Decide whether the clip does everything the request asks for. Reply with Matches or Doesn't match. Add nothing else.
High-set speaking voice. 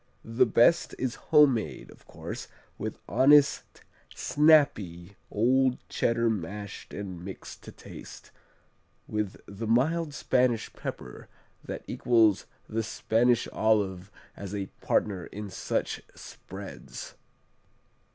Doesn't match